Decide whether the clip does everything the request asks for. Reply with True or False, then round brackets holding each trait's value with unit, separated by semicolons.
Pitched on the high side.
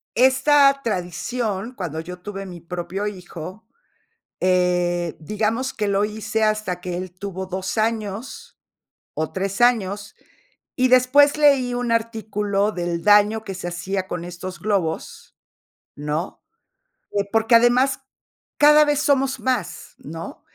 True (205 Hz)